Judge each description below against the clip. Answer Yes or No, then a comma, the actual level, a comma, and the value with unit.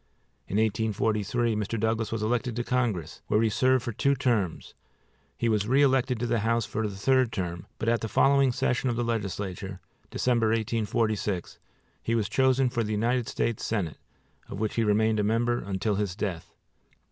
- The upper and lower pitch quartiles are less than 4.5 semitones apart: Yes, narrow, 2.6 semitones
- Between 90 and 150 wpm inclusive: No, average, 180 wpm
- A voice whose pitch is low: Yes, low, 110 Hz